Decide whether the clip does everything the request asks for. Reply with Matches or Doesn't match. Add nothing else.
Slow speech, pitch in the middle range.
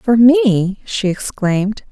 Doesn't match